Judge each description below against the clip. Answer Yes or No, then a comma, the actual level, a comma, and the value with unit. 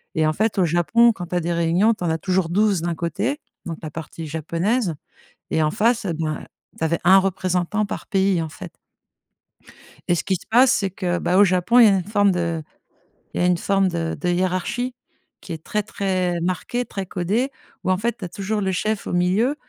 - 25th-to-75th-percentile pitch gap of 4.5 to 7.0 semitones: No, average, 3.4 semitones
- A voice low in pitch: No, medium, 185 Hz